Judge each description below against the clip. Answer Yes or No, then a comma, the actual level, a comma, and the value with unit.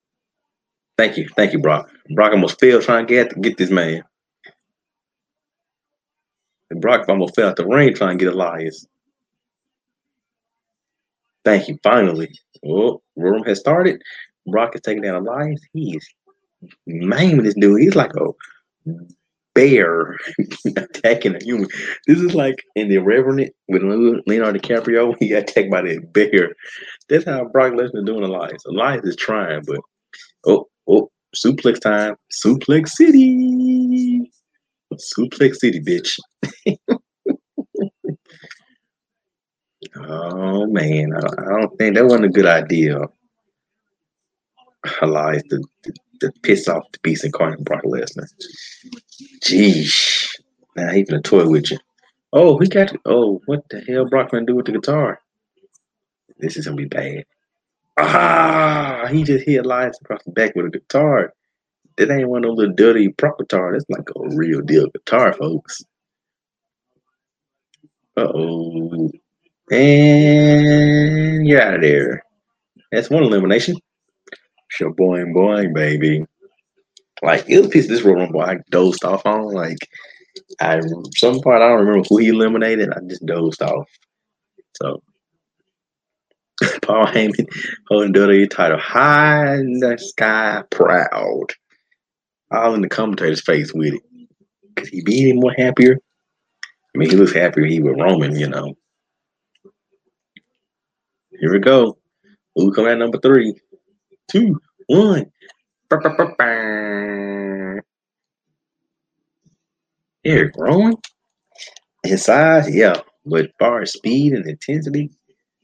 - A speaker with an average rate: No, slow, 130 wpm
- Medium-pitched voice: No, low, 130 Hz